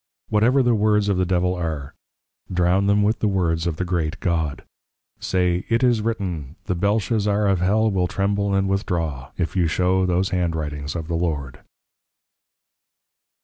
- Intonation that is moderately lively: Yes, average, 3.3 semitones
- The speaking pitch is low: Yes, very low, 90 Hz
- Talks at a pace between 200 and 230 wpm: No, average, 165 wpm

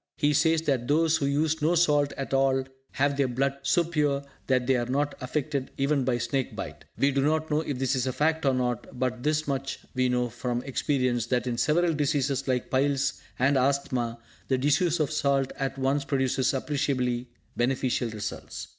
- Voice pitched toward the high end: No, low, 135 Hz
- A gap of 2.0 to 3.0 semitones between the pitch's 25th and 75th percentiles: Yes, narrow, 2.5 semitones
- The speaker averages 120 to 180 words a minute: No, average, 190 wpm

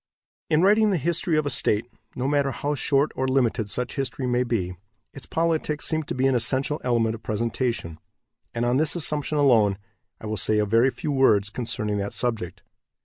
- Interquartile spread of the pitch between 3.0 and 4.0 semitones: No, average, 4.6 semitones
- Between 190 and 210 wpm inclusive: Yes, average, 195 wpm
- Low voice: Yes, low, 125 Hz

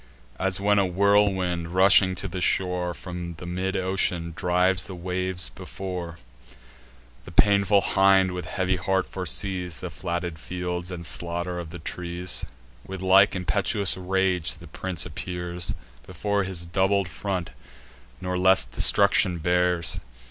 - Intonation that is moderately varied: No, narrow, 1.5 semitones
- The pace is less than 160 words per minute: Yes, slow, 135 wpm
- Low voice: Yes, very low, 90 Hz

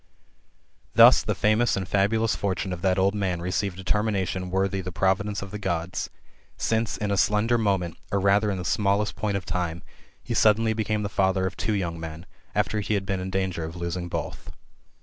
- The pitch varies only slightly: Yes, narrow, 2.3 semitones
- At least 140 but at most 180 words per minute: No, average, 200 wpm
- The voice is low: Yes, very low, 95 Hz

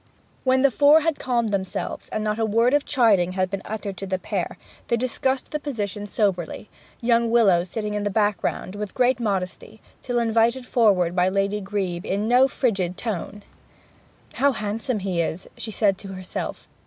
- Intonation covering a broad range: No, average, 3.7 semitones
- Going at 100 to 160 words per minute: No, average, 180 wpm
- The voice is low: No, high, 210 Hz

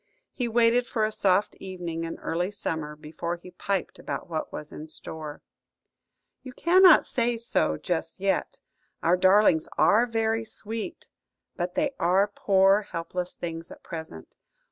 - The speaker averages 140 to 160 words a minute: Yes, average, 145 wpm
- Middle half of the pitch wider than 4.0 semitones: Yes, average, 5.2 semitones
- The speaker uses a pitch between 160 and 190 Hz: Yes, medium, 185 Hz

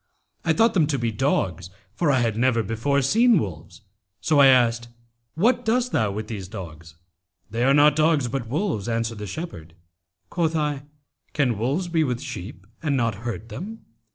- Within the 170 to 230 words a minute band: Yes, average, 180 wpm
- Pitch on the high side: No, low, 125 Hz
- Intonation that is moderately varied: No, wide, 6.1 semitones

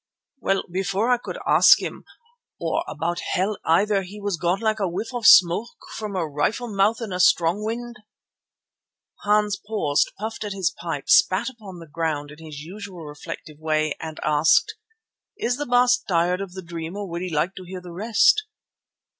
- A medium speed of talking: Yes, average, 180 wpm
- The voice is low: No, high, 190 Hz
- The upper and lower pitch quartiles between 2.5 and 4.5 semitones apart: Yes, average, 4.2 semitones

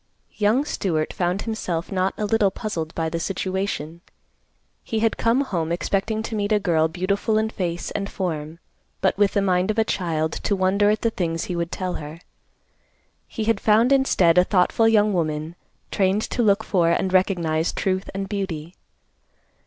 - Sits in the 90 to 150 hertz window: No, high, 190 Hz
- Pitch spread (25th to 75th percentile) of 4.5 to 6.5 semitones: No, average, 3.9 semitones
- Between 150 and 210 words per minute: Yes, average, 175 wpm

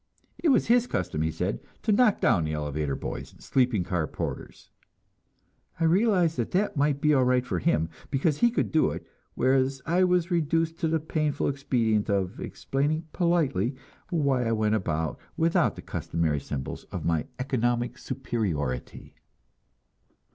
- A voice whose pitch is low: Yes, low, 130 Hz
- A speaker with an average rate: Yes, average, 160 wpm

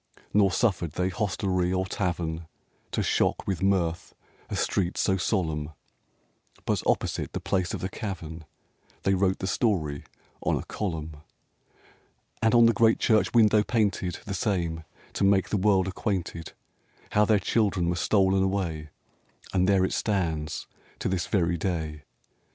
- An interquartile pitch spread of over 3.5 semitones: No, average, 3.0 semitones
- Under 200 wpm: Yes, average, 150 wpm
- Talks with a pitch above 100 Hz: No, very low, 95 Hz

